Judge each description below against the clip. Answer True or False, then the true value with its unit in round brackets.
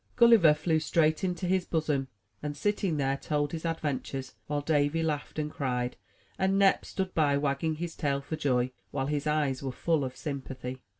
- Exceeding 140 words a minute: True (180 wpm)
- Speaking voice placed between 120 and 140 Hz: False (150 Hz)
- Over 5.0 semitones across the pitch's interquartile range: False (3.0 semitones)